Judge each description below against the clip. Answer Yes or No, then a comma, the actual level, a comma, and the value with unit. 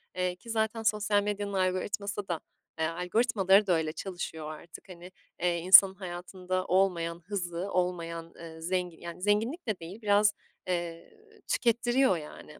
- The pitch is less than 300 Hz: Yes, medium, 185 Hz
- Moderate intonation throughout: Yes, average, 3.2 semitones